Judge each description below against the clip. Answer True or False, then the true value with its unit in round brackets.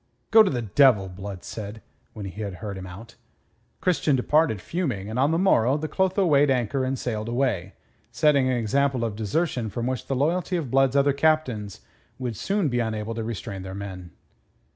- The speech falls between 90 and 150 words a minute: False (190 wpm)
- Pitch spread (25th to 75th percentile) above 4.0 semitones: True (5.3 semitones)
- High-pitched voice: False (125 Hz)